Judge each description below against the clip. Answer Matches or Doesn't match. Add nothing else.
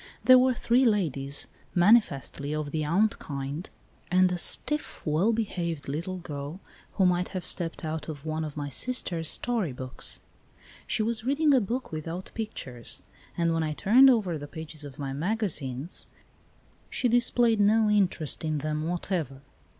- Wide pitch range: Matches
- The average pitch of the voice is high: Doesn't match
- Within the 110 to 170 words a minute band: Matches